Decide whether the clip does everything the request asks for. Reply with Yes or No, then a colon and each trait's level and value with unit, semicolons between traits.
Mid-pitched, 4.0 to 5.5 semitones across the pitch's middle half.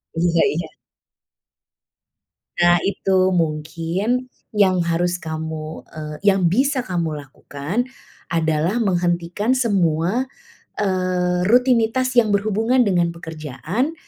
Yes: medium, 180 Hz; average, 4.6 semitones